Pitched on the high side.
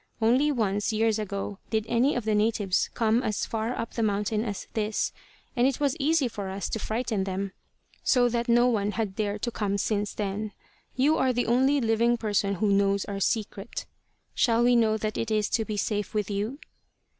Yes: high, 220 Hz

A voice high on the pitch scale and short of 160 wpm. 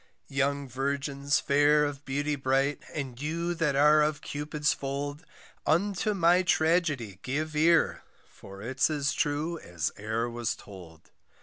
No: medium, 145 Hz; slow, 135 wpm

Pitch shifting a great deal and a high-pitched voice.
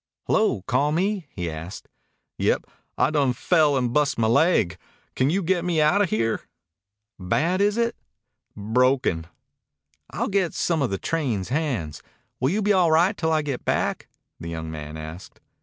No: wide, 8.9 semitones; medium, 140 Hz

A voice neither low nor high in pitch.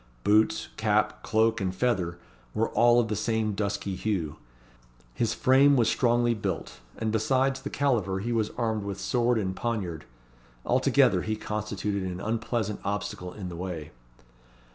No: low, 110 Hz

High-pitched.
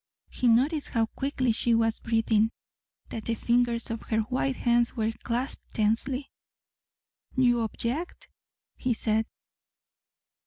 Yes: high, 235 Hz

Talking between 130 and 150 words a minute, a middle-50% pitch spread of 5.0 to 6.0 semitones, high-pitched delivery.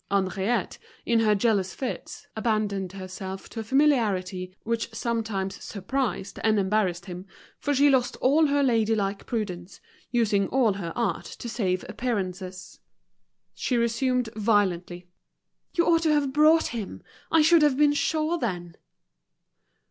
Yes: average, 140 wpm; average, 5.3 semitones; high, 220 Hz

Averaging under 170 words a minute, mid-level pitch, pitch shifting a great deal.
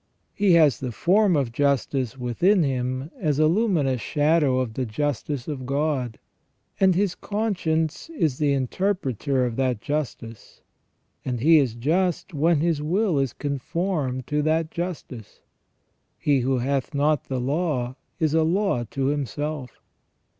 No: average, 145 wpm; medium, 145 Hz; average, 4.3 semitones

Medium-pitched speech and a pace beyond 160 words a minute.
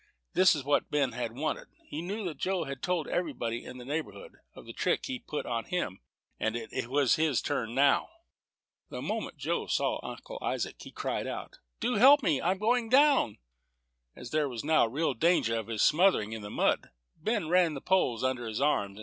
Yes: medium, 150 Hz; average, 200 wpm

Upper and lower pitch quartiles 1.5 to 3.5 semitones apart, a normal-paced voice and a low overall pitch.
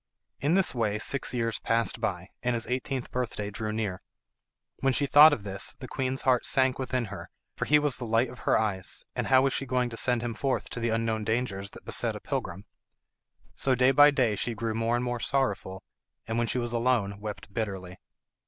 No: average, 3.2 semitones; fast, 210 wpm; low, 120 Hz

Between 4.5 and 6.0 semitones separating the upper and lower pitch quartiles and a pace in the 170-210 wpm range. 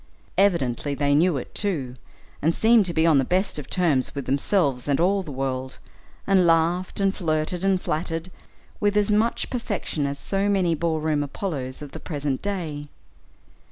Yes: average, 5.2 semitones; average, 175 wpm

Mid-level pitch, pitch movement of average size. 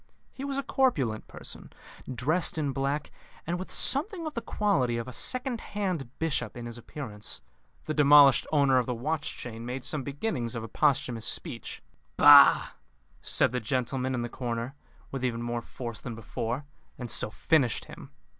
No: low, 130 Hz; average, 4.9 semitones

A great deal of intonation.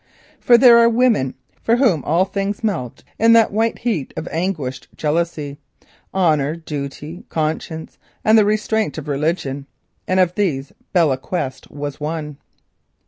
Yes: wide, 6.4 semitones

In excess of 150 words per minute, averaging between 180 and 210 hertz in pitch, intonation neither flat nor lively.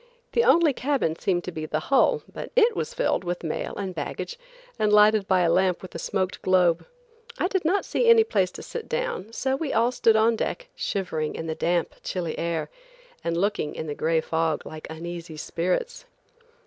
No: average, 200 wpm; high, 190 Hz; wide, 8.9 semitones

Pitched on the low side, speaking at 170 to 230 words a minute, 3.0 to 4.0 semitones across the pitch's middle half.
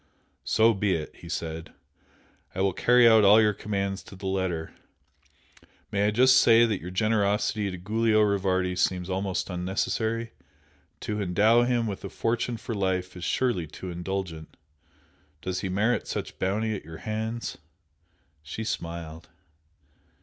No: low, 100 Hz; average, 150 wpm; average, 3.3 semitones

